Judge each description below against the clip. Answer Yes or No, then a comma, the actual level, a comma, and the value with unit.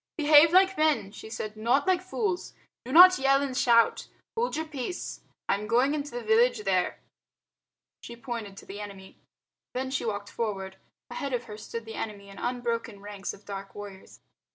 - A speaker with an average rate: Yes, average, 180 wpm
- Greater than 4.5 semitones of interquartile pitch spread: Yes, wide, 5.6 semitones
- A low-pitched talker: No, high, 235 Hz